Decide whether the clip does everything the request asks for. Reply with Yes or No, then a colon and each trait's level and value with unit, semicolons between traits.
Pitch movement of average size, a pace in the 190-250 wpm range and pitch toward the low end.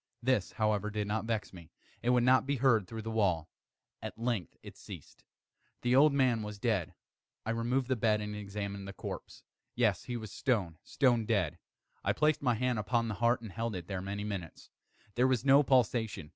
Yes: average, 3.4 semitones; average, 200 wpm; low, 110 Hz